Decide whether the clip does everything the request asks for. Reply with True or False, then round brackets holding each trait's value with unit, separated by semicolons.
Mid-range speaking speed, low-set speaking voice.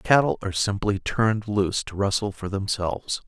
True (185 wpm; 100 Hz)